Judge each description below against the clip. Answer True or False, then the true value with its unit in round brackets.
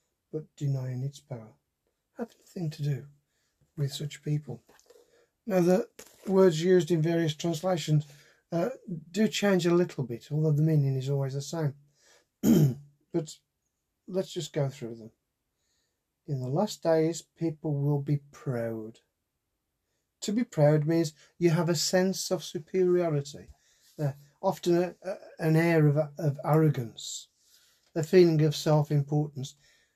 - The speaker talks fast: False (135 wpm)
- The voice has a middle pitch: True (155 Hz)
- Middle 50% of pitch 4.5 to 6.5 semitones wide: False (3.5 semitones)